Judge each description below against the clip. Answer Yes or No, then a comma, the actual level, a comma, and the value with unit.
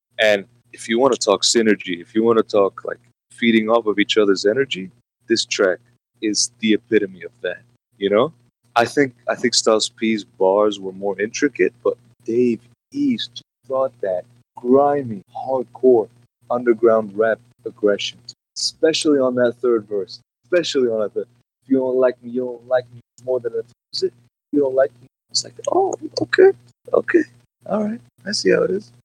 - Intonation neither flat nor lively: Yes, average, 3.2 semitones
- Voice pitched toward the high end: No, low, 120 Hz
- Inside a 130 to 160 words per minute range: No, average, 175 wpm